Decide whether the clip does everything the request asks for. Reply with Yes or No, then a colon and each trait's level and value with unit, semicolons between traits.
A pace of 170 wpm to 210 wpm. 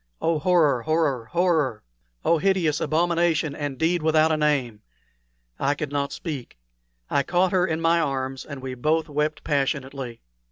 No: average, 155 wpm